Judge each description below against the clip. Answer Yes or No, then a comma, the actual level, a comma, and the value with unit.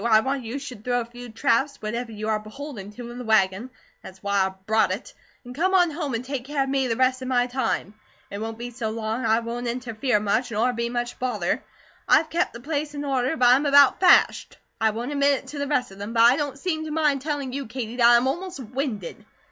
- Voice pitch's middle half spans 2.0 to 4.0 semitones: Yes, average, 3.7 semitones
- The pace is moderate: No, fast, 250 wpm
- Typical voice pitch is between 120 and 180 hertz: No, high, 245 Hz